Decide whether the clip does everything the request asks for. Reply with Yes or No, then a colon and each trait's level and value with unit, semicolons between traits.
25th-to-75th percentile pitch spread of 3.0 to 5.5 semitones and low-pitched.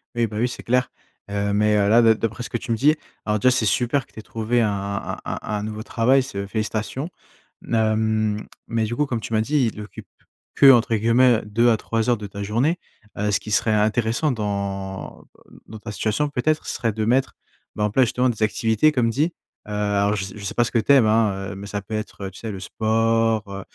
No: narrow, 2.4 semitones; low, 110 Hz